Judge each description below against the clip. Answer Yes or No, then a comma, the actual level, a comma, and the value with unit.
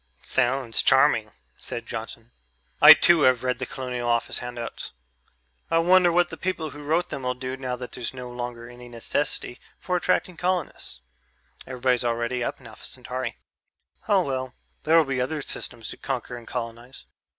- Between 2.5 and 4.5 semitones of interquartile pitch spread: Yes, average, 3.4 semitones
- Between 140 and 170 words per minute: Yes, average, 160 wpm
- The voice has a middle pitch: No, low, 125 Hz